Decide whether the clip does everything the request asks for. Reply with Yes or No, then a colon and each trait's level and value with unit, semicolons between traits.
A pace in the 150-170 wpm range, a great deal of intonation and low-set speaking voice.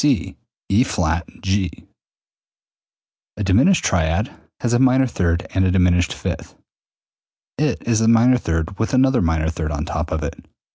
Yes: average, 155 wpm; wide, 6.3 semitones; very low, 95 Hz